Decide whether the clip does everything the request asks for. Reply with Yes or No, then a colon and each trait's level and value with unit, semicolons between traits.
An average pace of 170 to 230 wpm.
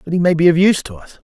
No: fast, 365 wpm